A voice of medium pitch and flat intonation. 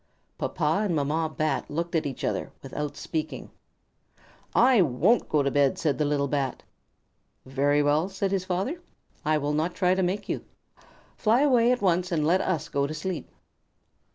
No: medium, 160 Hz; average, 4.4 semitones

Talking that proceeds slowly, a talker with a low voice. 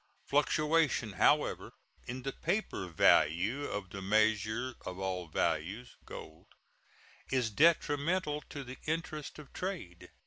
Yes: slow, 115 wpm; low, 125 Hz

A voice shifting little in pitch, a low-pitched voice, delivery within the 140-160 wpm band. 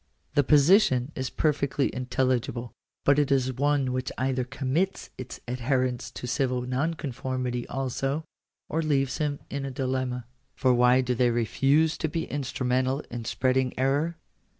Yes: narrow, 2.1 semitones; low, 130 Hz; average, 145 wpm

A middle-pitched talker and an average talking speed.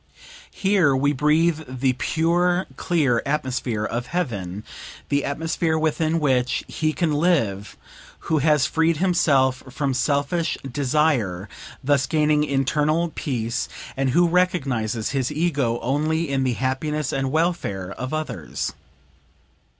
No: medium, 145 Hz; slow, 120 wpm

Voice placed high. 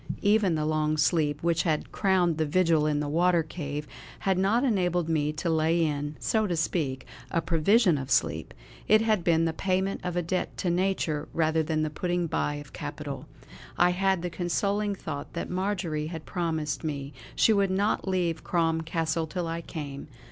No: medium, 165 Hz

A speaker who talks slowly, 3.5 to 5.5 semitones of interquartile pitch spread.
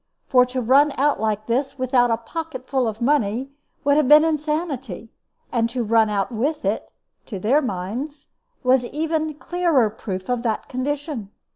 No: average, 165 wpm; average, 4.5 semitones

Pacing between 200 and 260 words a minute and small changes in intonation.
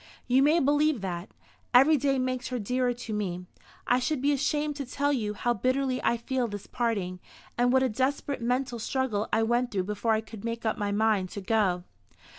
No: fast, 205 wpm; average, 3.8 semitones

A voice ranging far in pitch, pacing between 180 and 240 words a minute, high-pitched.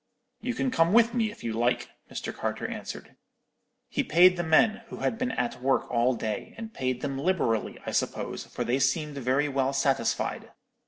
No: wide, 8.4 semitones; average, 190 wpm; medium, 140 Hz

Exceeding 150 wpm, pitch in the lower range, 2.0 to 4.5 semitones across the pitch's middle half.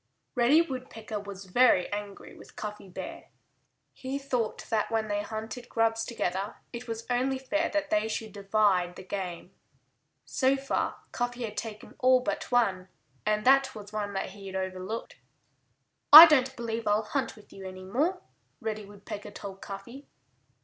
No: average, 165 wpm; high, 220 Hz; average, 4.0 semitones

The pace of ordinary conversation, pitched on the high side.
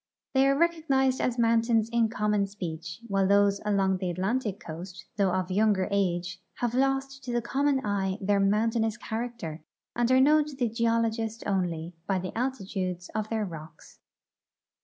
Yes: average, 160 wpm; high, 210 Hz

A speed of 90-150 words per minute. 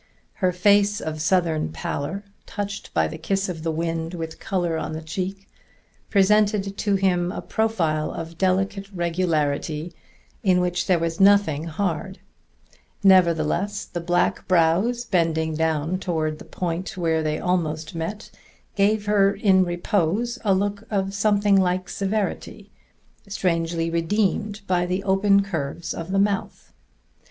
Yes: average, 140 wpm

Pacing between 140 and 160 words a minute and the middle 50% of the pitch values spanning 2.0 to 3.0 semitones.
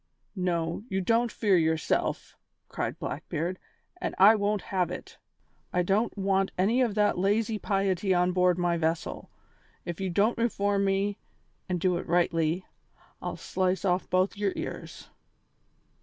Yes: average, 145 wpm; narrow, 2.4 semitones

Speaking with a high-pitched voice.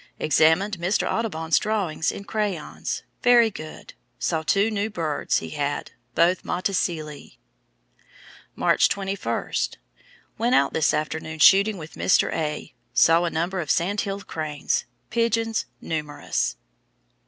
No: medium, 175 Hz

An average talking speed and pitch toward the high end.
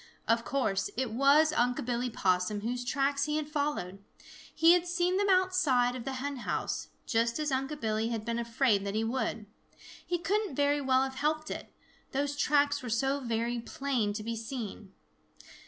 Yes: average, 180 wpm; very high, 260 Hz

